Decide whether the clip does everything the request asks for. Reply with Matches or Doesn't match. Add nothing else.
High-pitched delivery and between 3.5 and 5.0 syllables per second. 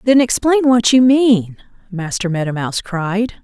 Matches